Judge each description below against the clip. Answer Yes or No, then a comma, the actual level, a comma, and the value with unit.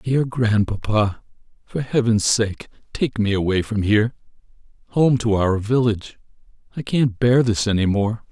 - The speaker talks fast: No, average, 145 wpm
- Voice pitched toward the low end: Yes, low, 110 Hz